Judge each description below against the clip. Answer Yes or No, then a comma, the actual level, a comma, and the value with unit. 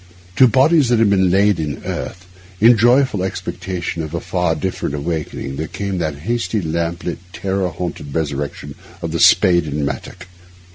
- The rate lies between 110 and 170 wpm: Yes, average, 165 wpm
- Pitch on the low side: Yes, very low, 90 Hz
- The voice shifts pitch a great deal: No, average, 4.3 semitones